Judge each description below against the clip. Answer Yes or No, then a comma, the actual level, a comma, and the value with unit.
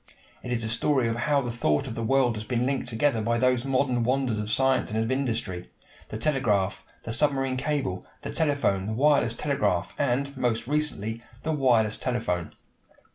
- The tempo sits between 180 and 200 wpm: Yes, average, 185 wpm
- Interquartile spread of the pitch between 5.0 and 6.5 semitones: No, average, 3.5 semitones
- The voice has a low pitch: Yes, low, 120 Hz